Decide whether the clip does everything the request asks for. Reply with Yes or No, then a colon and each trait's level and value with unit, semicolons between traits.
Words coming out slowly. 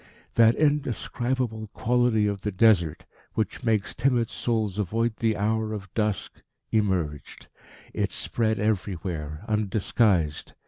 Yes: slow, 110 wpm